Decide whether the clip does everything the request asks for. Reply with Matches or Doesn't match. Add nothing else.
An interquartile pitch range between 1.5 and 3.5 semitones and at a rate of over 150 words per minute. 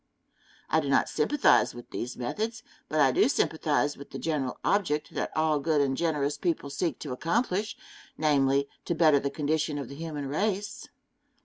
Matches